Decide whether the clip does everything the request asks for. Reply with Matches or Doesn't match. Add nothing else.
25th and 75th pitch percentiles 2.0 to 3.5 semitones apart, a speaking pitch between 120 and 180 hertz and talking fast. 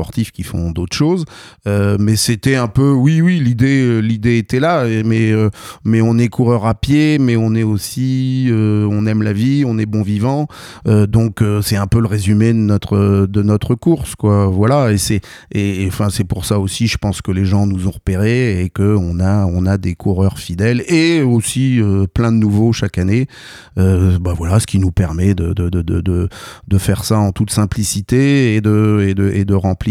Doesn't match